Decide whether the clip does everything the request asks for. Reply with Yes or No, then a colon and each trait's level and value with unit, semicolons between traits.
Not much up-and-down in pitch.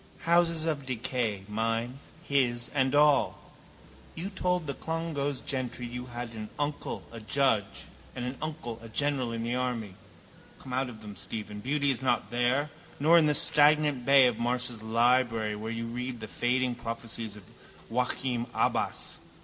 No: average, 3.5 semitones